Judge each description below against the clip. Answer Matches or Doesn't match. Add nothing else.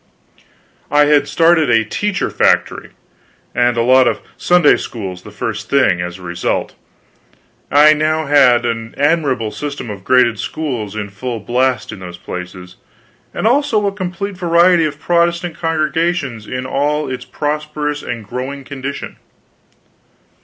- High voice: Doesn't match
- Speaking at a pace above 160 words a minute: Doesn't match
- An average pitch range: Doesn't match